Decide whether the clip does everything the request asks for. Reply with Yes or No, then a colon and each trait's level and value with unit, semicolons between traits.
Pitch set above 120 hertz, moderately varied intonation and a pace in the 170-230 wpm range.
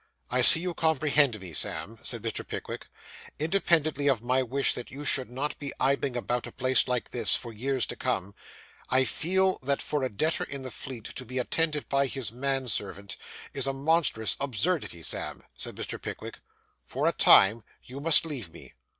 Yes: low, 135 Hz; average, 3.3 semitones; average, 185 wpm